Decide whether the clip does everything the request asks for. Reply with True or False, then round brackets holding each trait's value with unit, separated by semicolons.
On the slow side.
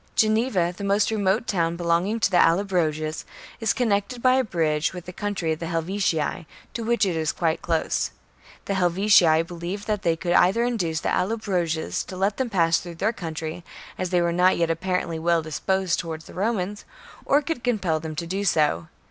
False (195 wpm)